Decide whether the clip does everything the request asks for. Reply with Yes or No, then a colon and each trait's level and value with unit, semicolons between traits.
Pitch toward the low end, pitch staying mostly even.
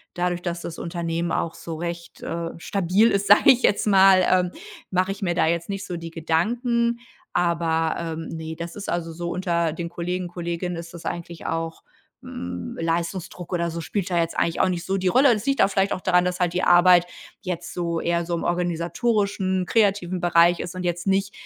No: medium, 175 Hz; narrow, 1.9 semitones